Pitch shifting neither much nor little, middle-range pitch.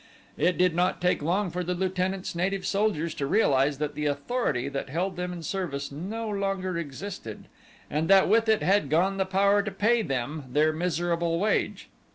Yes: average, 4.3 semitones; medium, 180 Hz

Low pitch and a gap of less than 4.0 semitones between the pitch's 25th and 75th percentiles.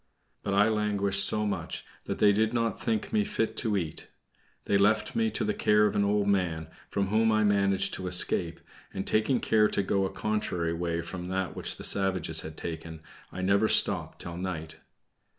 Yes: low, 100 Hz; average, 3.2 semitones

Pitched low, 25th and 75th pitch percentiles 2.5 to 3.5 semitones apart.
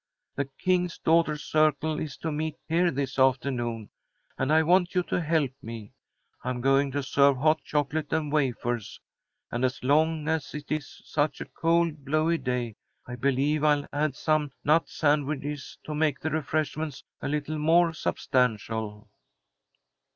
No: medium, 150 Hz; average, 2.9 semitones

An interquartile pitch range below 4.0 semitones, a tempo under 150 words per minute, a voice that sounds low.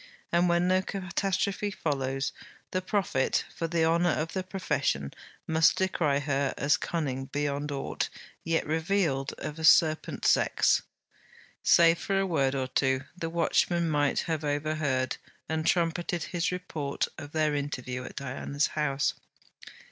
No: average, 3.6 semitones; average, 140 wpm; medium, 155 Hz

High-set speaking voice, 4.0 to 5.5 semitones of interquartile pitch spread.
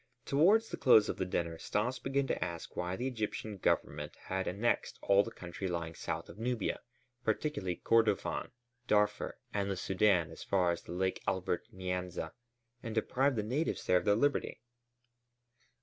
No: low, 100 Hz; average, 4.7 semitones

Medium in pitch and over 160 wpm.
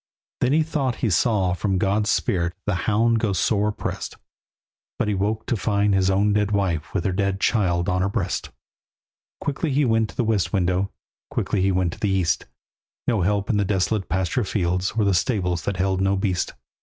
No: low, 100 Hz; average, 200 wpm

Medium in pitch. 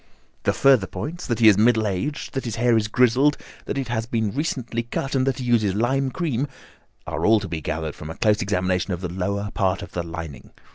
No: low, 110 Hz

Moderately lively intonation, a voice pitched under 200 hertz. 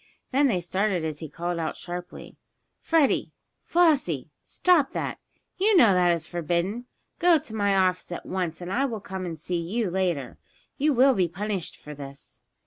No: wide, 6.3 semitones; medium, 185 Hz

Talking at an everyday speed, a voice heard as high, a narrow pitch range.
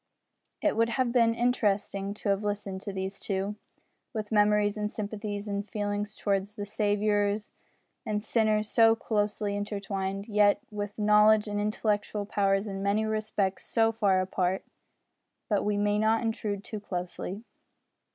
Yes: average, 145 wpm; high, 205 Hz; narrow, 1.2 semitones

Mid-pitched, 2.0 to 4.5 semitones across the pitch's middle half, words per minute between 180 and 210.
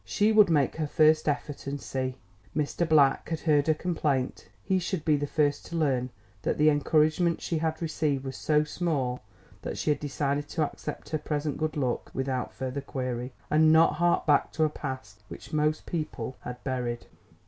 Yes: medium, 150 Hz; average, 2.7 semitones; average, 190 wpm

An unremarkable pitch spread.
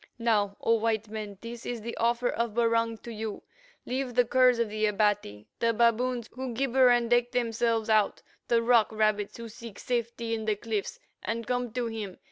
No: narrow, 1.8 semitones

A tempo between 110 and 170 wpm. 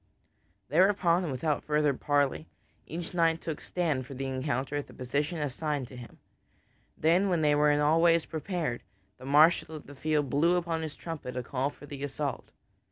No: average, 185 wpm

